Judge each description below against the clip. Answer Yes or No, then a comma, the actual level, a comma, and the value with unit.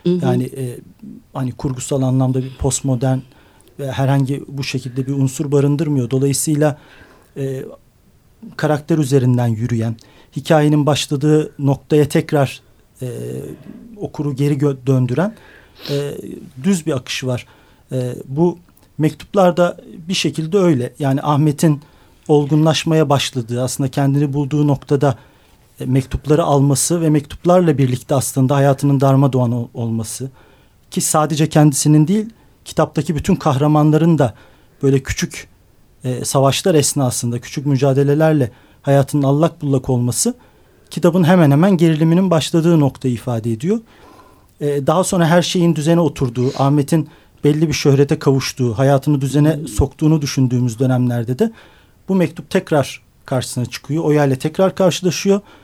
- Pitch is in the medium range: Yes, medium, 145 Hz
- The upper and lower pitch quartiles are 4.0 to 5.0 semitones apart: No, average, 3.2 semitones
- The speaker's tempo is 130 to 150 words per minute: No, average, 115 wpm